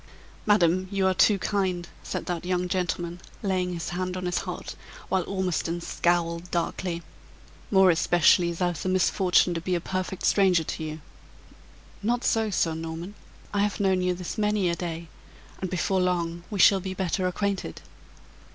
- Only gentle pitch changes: Yes, narrow, 1.8 semitones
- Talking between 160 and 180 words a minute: Yes, average, 170 wpm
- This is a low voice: No, medium, 180 Hz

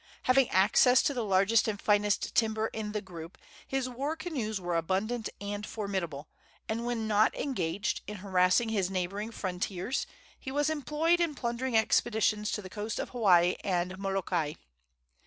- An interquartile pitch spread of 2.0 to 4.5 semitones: Yes, average, 4.2 semitones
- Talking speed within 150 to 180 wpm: Yes, average, 155 wpm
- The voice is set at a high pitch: Yes, high, 210 Hz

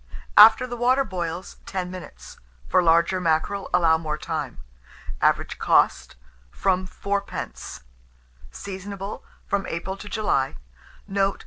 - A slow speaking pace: Yes, slow, 115 wpm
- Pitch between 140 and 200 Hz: Yes, high, 190 Hz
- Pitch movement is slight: No, average, 3.0 semitones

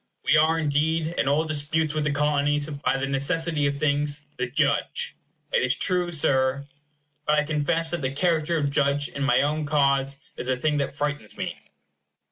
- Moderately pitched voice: Yes, medium, 145 Hz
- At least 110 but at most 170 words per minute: No, average, 185 wpm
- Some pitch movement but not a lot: No, narrow, 1.8 semitones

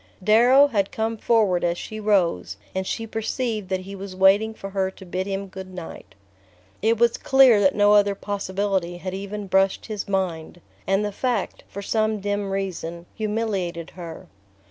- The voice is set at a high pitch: Yes, high, 200 Hz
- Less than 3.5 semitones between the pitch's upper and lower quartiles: Yes, narrow, 2.5 semitones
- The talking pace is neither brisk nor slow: Yes, average, 170 wpm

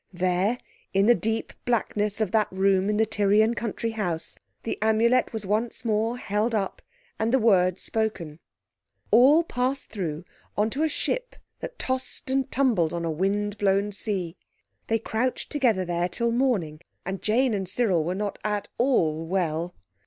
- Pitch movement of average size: Yes, average, 3.9 semitones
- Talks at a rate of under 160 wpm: No, average, 165 wpm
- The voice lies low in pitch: No, high, 210 Hz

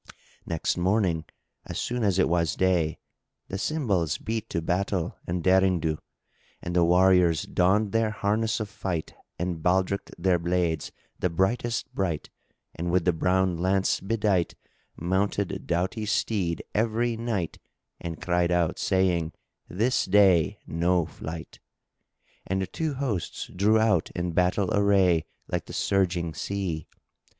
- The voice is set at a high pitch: No, very low, 95 Hz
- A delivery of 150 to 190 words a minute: No, average, 140 wpm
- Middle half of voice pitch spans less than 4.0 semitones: Yes, average, 2.9 semitones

